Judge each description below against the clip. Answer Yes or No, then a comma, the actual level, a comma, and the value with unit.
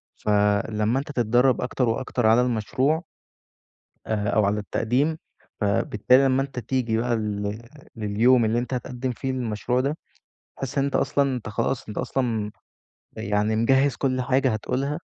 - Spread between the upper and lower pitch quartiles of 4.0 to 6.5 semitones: No, average, 3.6 semitones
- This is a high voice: No, low, 120 Hz